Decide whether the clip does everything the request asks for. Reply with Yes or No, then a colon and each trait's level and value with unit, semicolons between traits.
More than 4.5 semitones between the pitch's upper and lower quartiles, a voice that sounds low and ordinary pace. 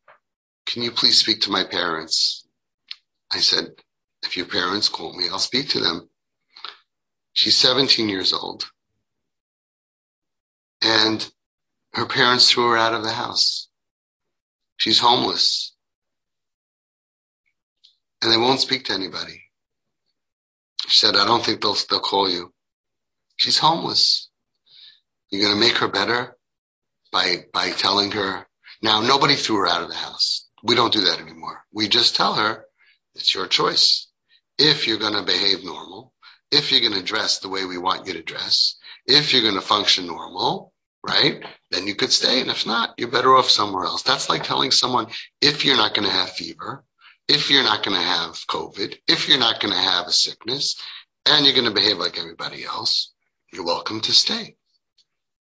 Yes: average, 5.2 semitones; low, 120 Hz; average, 165 wpm